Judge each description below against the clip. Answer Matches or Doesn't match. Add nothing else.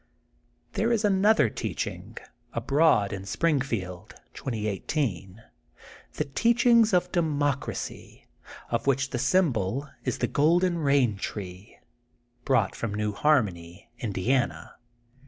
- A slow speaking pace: Matches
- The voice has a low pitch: Matches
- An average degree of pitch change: Doesn't match